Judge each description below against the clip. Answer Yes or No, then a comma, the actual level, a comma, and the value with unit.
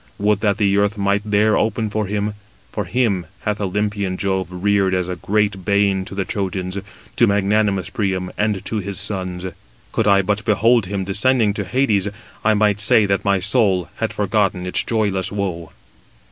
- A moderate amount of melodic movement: No, narrow, 1.8 semitones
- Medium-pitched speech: No, low, 100 Hz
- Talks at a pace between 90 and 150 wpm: No, average, 175 wpm